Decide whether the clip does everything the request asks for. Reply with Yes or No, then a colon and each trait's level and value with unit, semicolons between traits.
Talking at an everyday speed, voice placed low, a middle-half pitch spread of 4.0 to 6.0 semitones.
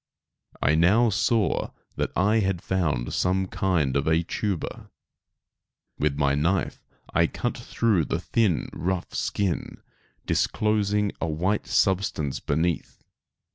No: slow, 120 wpm; very low, 90 Hz; average, 4.5 semitones